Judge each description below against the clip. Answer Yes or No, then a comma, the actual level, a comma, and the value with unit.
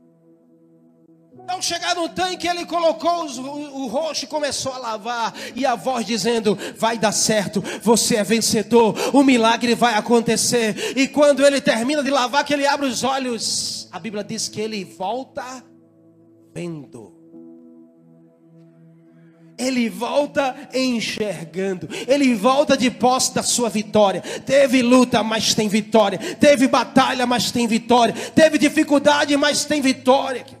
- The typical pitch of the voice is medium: No, high, 235 Hz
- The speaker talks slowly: No, average, 140 wpm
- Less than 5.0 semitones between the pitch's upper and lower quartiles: No, wide, 5.5 semitones